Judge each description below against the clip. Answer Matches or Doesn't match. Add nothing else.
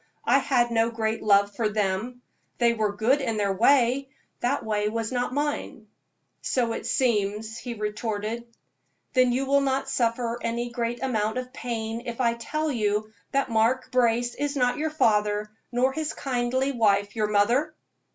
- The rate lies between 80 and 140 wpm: Doesn't match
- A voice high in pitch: Matches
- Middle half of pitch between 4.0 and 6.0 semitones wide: Doesn't match